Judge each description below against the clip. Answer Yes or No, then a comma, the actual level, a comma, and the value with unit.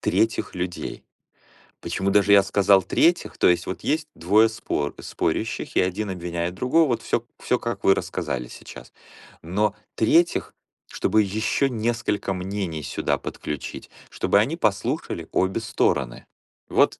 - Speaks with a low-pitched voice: Yes, low, 100 Hz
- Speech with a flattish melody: No, average, 3.8 semitones